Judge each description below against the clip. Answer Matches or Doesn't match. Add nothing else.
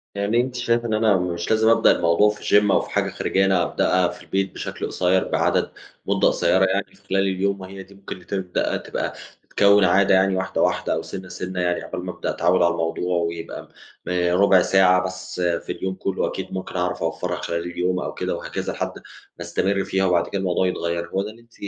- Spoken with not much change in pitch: Matches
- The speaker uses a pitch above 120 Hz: Doesn't match